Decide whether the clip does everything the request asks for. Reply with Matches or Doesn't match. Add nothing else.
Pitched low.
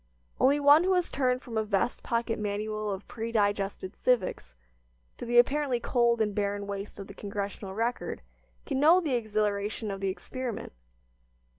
Doesn't match